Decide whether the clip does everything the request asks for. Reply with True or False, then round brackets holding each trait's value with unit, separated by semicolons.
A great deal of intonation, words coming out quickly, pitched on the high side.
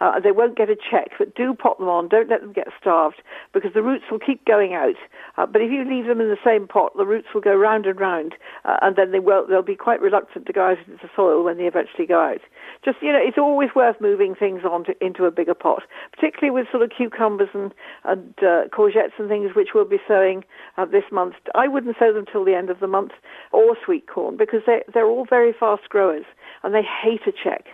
True (5.8 semitones; 255 wpm; 220 Hz)